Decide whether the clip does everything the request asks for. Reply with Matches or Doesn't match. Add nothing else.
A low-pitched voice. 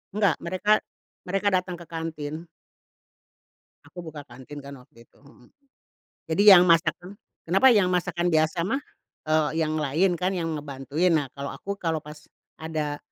Doesn't match